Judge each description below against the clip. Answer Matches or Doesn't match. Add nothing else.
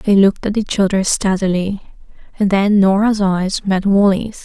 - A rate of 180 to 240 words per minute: Doesn't match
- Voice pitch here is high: Matches